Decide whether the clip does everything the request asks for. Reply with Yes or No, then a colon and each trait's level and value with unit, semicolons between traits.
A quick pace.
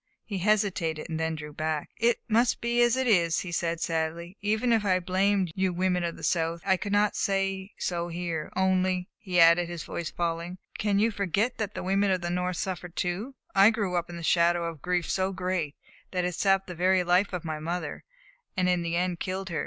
Yes: fast, 225 wpm